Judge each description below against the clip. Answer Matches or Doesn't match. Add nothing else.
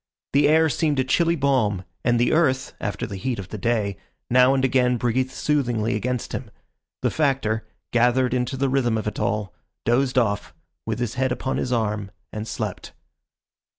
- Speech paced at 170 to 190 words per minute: Matches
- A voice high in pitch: Doesn't match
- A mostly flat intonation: Doesn't match